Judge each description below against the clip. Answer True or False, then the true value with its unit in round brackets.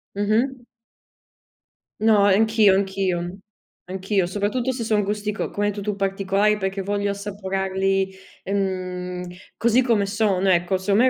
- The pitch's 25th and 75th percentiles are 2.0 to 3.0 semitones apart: False (1.6 semitones)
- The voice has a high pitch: True (200 Hz)